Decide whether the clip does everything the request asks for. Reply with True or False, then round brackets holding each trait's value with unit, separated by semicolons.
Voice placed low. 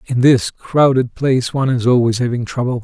True (125 Hz)